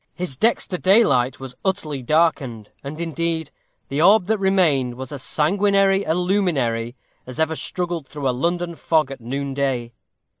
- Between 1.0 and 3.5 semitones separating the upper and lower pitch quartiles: No, average, 5.2 semitones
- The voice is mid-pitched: Yes, medium, 155 Hz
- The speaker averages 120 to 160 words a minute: Yes, average, 150 wpm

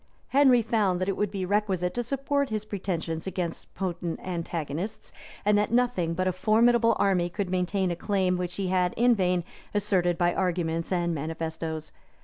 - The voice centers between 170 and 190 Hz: Yes, medium, 185 Hz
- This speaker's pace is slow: No, average, 170 wpm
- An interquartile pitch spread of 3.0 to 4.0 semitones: Yes, average, 3.3 semitones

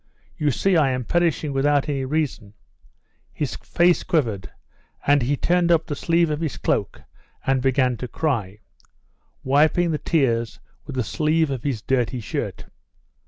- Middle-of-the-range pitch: Yes, medium, 145 Hz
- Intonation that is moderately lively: Yes, average, 3.9 semitones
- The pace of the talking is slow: No, average, 155 wpm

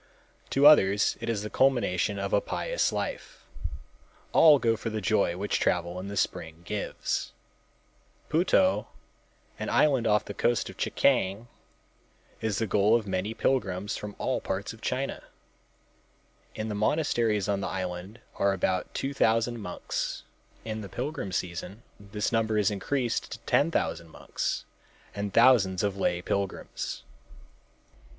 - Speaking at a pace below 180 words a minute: Yes, average, 145 wpm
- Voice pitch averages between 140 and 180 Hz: No, low, 105 Hz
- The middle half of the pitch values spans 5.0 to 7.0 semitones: No, average, 3.6 semitones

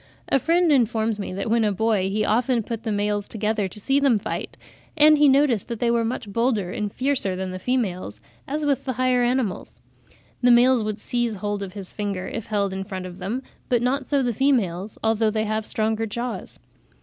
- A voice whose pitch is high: Yes, high, 225 Hz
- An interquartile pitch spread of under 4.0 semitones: Yes, average, 3.6 semitones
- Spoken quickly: Yes, fast, 210 wpm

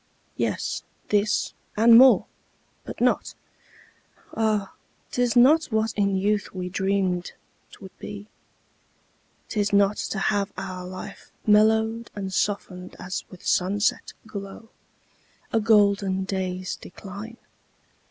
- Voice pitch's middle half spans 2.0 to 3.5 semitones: Yes, narrow, 2.4 semitones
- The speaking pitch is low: No, high, 200 Hz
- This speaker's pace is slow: Yes, slow, 110 wpm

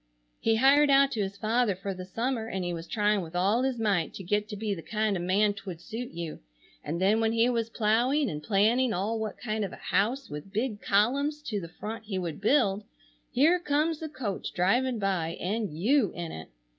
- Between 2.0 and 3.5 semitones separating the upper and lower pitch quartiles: No, average, 4.3 semitones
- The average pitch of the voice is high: Yes, high, 215 Hz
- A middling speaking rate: No, fast, 220 wpm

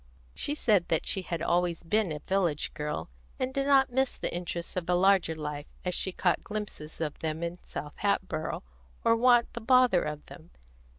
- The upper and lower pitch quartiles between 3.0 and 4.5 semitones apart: No, average, 5.3 semitones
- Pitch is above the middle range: No, medium, 180 Hz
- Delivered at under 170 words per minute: No, average, 190 wpm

